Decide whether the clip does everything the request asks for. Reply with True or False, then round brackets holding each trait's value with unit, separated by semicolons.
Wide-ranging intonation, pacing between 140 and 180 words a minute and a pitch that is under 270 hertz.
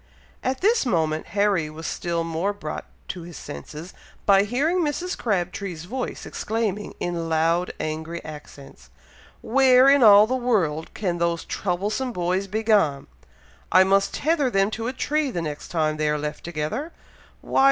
True (6.4 semitones; 160 wpm; 190 Hz)